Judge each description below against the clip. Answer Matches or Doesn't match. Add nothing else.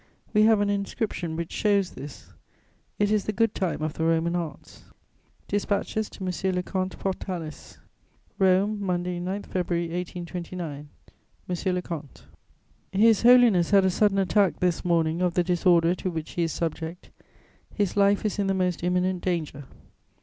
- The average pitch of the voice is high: Doesn't match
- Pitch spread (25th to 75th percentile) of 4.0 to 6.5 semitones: Doesn't match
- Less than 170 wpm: Matches